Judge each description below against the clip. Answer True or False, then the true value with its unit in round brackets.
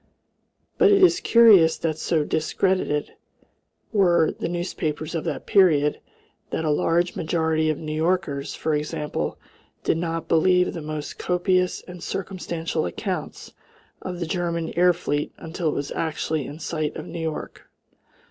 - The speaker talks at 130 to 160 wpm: True (150 wpm)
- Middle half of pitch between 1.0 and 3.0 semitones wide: True (2.5 semitones)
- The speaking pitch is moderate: True (165 Hz)